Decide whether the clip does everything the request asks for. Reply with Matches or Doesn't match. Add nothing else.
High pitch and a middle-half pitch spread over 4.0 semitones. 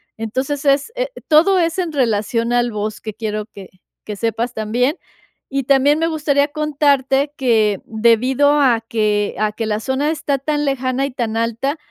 Matches